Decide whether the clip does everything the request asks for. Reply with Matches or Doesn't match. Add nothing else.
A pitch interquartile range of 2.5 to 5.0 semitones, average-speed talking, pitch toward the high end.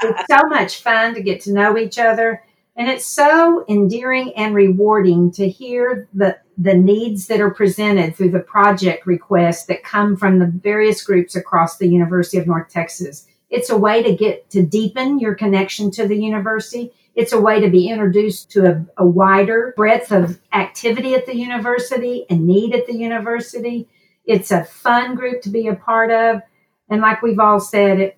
Matches